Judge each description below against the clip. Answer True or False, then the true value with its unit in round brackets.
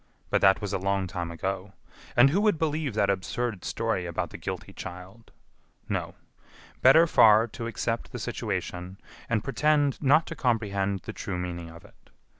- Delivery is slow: False (170 wpm)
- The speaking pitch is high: False (105 Hz)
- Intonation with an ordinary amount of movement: False (5.9 semitones)